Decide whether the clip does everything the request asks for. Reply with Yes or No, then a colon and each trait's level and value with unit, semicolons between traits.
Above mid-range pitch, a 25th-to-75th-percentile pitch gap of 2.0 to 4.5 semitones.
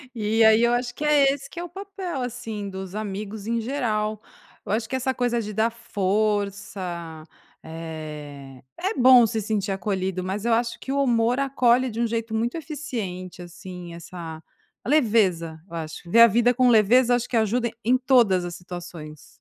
No: high, 220 Hz; average, 4.9 semitones